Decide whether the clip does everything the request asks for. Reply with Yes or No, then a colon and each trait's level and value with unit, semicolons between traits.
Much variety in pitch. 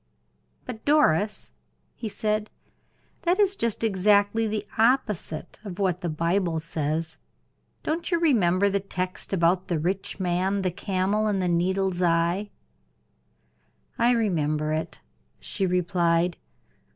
No: average, 3.7 semitones